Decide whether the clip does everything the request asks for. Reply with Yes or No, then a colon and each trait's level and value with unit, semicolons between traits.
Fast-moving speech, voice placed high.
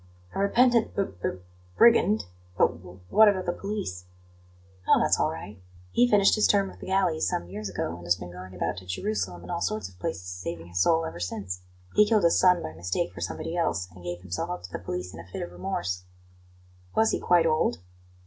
No: fast, 220 wpm; very low, 95 Hz